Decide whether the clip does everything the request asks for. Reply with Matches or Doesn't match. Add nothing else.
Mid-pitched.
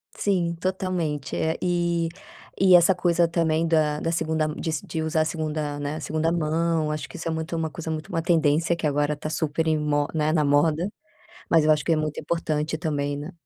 Matches